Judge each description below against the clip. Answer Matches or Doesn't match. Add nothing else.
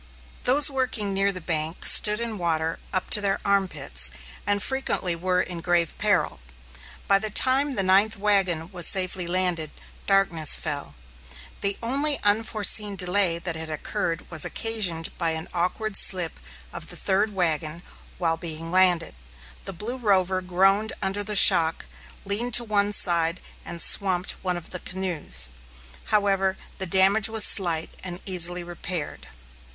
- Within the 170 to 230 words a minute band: Doesn't match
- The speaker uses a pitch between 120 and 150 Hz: Doesn't match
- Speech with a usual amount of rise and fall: Matches